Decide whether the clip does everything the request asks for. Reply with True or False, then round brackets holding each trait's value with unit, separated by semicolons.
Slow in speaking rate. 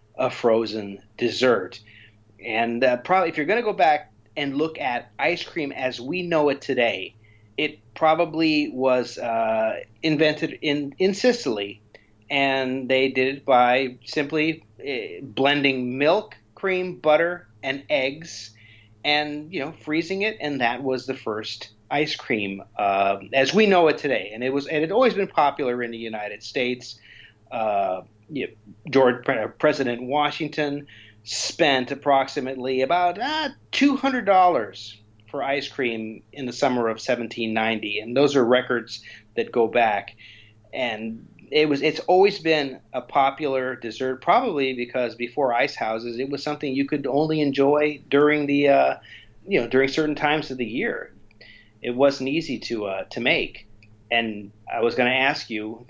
False (160 wpm)